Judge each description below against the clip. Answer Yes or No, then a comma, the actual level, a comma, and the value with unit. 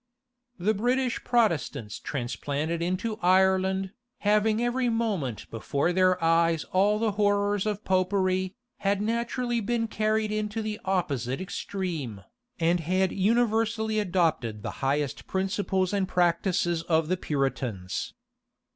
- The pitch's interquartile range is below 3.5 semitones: No, average, 4.4 semitones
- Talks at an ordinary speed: No, slow, 120 wpm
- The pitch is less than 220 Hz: Yes, high, 190 Hz